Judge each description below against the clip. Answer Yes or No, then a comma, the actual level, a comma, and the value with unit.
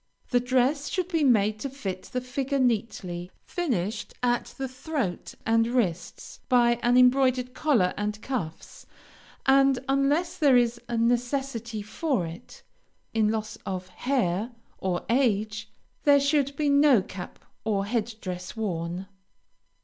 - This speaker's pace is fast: No, average, 140 wpm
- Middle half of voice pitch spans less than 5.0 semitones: Yes, average, 4.6 semitones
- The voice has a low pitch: No, high, 240 Hz